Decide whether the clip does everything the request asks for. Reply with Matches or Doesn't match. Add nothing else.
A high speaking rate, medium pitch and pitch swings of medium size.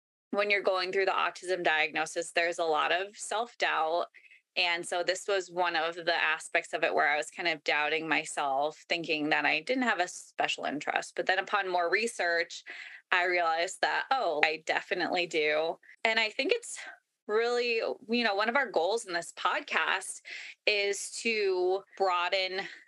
Doesn't match